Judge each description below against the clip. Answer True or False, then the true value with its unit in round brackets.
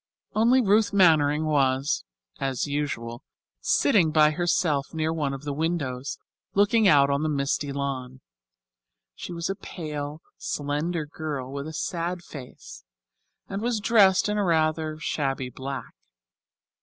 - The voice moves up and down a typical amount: True (4.0 semitones)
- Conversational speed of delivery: False (130 wpm)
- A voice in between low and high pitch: True (150 Hz)